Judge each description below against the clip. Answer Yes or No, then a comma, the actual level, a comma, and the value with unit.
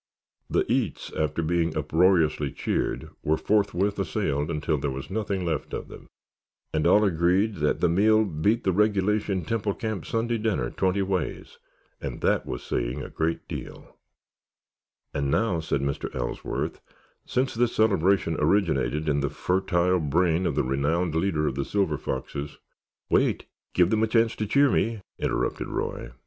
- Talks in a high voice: No, very low, 90 Hz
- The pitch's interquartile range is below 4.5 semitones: No, average, 5.2 semitones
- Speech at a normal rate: Yes, average, 160 wpm